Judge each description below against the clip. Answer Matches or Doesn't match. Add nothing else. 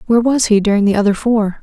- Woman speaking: Matches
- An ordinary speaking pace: Doesn't match